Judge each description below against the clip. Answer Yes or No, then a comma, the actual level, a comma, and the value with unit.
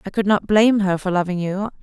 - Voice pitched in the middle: No, high, 195 Hz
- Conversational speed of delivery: No, fast, 265 wpm